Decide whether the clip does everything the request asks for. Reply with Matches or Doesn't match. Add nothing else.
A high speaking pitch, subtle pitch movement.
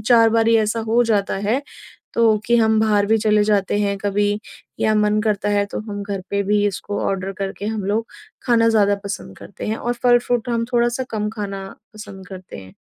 Matches